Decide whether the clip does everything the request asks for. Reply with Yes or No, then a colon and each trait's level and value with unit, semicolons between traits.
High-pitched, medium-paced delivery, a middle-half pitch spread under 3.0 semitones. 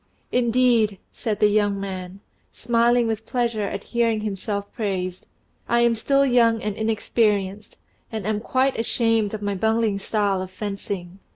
Yes: high, 215 Hz; average, 150 wpm; narrow, 2.6 semitones